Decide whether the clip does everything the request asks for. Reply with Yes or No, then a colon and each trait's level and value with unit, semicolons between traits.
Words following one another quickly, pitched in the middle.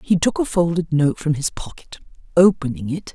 No: average, 190 wpm; medium, 165 Hz